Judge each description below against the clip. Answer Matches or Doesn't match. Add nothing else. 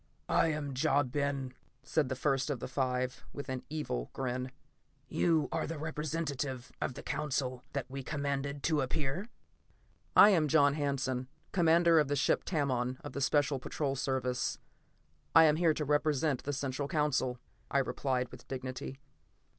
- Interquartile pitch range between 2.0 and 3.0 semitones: Matches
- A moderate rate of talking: Matches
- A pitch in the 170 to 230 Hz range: Doesn't match